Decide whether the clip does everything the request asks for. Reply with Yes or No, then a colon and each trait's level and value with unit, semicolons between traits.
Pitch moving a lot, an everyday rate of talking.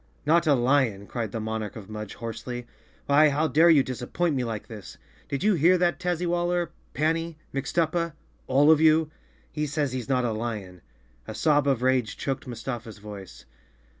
Yes: wide, 5.9 semitones; average, 165 wpm